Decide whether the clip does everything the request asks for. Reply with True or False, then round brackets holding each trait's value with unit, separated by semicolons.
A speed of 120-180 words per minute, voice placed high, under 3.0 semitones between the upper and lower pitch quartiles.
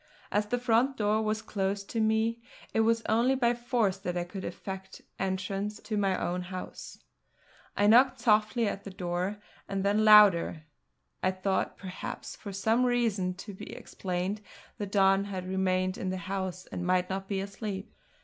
True (170 wpm; 200 Hz; 2.6 semitones)